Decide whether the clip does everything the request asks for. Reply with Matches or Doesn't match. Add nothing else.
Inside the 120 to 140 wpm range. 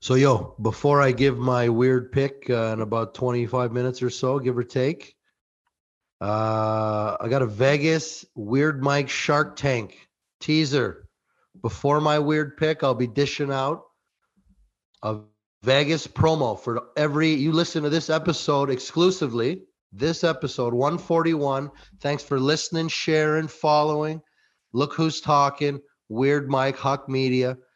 Matches